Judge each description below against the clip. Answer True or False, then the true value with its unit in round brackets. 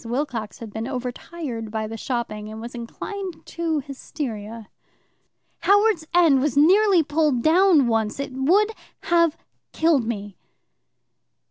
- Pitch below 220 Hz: False (270 Hz)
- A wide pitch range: True (6.6 semitones)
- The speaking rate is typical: False (125 wpm)